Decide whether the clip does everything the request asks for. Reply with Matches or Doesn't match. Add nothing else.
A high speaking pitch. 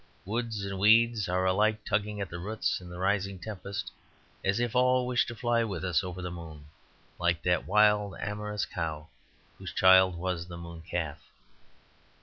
Doesn't match